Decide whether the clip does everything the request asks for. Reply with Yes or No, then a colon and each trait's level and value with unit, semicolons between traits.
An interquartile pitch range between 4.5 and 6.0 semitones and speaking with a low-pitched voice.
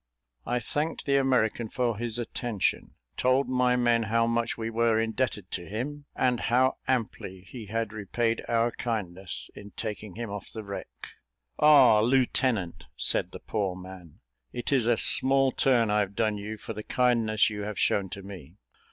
No: average, 3.2 semitones; low, 115 Hz